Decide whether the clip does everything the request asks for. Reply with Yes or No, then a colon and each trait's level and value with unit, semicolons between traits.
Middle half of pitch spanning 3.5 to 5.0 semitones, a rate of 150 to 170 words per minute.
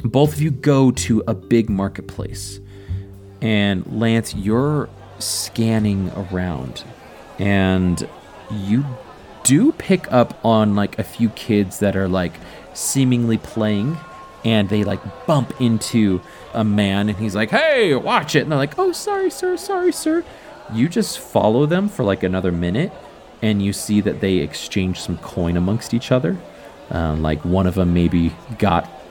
Yes: average, 3.9 semitones; average, 155 wpm